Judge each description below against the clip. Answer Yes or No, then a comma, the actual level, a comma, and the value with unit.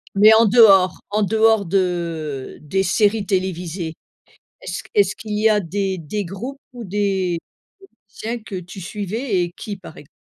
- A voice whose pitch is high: Yes, high, 195 Hz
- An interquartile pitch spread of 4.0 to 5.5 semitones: No, average, 3.1 semitones